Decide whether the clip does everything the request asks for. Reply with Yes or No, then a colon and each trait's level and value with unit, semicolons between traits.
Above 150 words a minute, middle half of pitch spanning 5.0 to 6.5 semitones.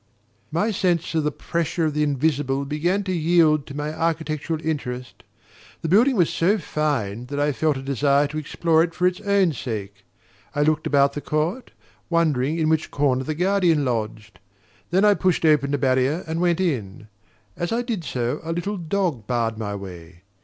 No: average, 185 wpm; average, 4.2 semitones